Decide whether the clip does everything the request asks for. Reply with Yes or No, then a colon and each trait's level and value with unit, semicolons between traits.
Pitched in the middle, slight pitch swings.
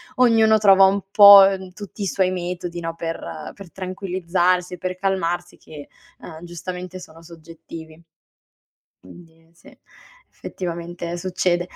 Yes: medium, 180 Hz; narrow, 2.2 semitones